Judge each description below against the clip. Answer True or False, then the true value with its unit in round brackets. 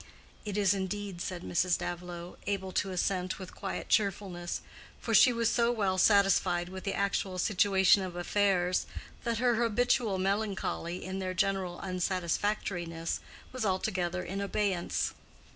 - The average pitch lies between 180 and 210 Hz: True (190 Hz)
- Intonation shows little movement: True (2.2 semitones)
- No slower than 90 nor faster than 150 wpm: True (140 wpm)